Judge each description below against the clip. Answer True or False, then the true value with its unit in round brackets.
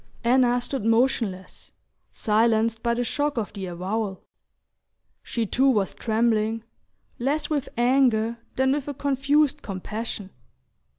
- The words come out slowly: True (120 wpm)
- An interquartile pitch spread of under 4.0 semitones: True (3.5 semitones)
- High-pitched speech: True (235 Hz)